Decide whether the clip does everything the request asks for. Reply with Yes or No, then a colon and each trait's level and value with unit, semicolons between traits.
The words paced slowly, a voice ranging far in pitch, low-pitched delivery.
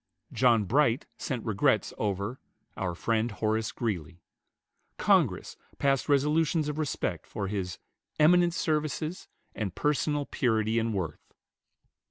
Yes: slow, 115 wpm; wide, 6.3 semitones; low, 115 Hz